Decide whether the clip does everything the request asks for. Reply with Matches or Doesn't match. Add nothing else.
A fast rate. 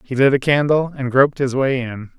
Matches